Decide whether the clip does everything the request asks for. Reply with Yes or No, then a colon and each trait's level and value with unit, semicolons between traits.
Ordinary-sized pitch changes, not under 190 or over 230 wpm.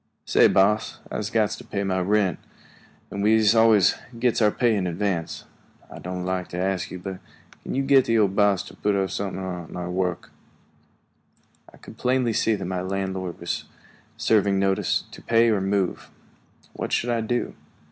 No: average, 3.0 semitones; average, 180 wpm